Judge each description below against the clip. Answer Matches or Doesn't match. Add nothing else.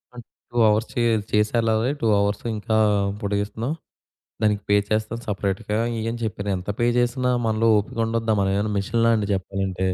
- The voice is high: Doesn't match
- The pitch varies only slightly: Matches